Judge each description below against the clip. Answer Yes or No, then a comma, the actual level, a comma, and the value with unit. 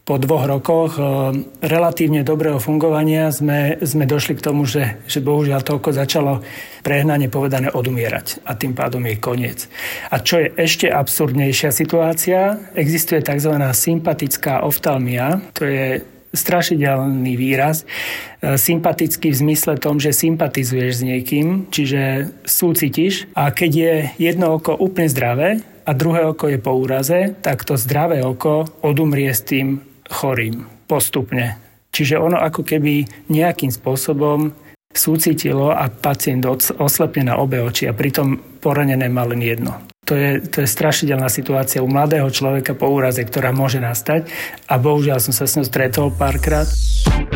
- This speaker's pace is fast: No, average, 140 wpm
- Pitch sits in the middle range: Yes, medium, 145 Hz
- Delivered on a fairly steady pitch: No, average, 3.0 semitones